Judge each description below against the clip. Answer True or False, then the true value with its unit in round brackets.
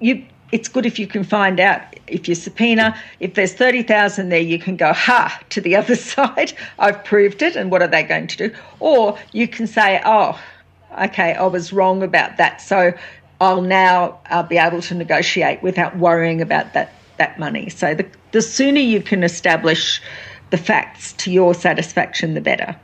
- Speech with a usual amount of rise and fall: True (3.7 semitones)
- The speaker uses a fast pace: False (190 wpm)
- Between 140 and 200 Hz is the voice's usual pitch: True (190 Hz)